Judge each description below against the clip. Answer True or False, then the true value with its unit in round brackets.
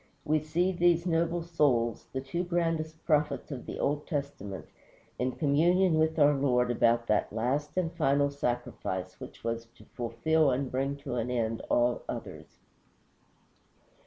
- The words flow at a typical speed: True (150 wpm)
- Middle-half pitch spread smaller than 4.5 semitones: False (4.8 semitones)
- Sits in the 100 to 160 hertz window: True (140 Hz)